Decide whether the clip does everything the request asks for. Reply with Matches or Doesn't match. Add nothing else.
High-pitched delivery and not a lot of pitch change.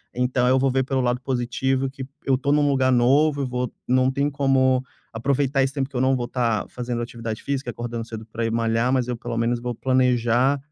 Doesn't match